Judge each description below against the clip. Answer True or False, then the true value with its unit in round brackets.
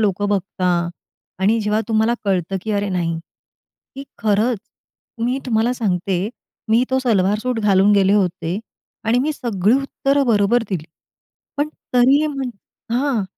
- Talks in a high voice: True (215 Hz)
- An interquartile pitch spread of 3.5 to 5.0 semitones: True (4.1 semitones)